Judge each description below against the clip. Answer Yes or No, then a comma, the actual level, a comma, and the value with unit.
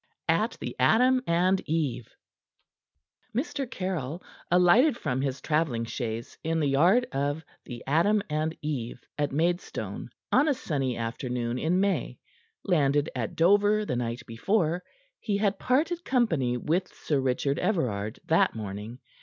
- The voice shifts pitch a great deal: Yes, wide, 7.3 semitones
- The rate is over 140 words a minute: No, slow, 135 wpm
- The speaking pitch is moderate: Yes, medium, 155 Hz